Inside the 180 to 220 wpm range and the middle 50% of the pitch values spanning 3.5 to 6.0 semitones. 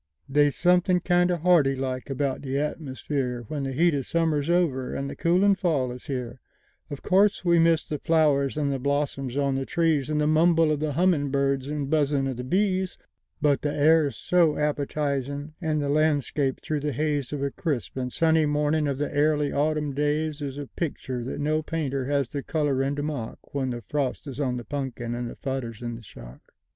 No: average, 185 wpm; narrow, 2.6 semitones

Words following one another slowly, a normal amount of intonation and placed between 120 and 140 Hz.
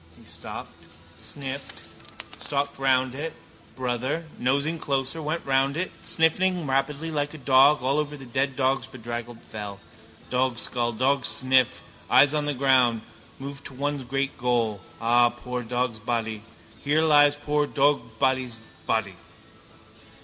Yes: slow, 130 wpm; average, 3.0 semitones; low, 135 Hz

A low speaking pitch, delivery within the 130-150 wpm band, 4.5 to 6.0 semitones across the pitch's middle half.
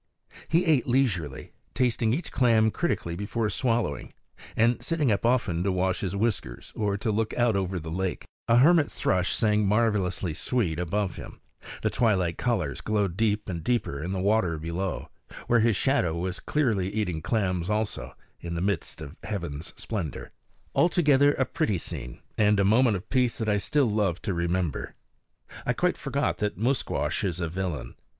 No: low, 105 Hz; average, 170 wpm; average, 4.8 semitones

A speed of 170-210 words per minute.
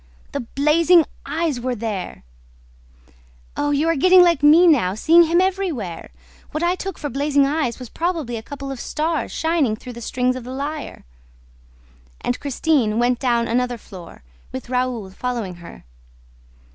No: average, 160 wpm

